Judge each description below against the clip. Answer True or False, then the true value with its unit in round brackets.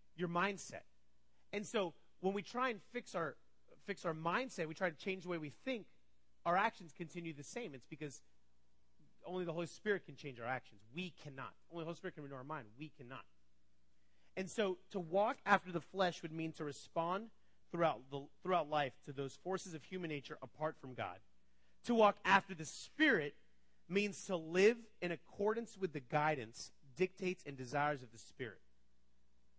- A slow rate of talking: False (185 wpm)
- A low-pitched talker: False (160 Hz)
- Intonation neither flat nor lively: False (6.7 semitones)